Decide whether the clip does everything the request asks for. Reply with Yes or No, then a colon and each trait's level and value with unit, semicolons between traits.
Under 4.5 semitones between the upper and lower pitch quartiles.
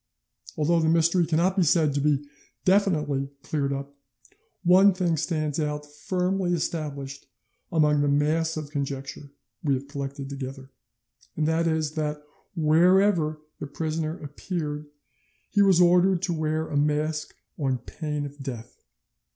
Yes: average, 2.7 semitones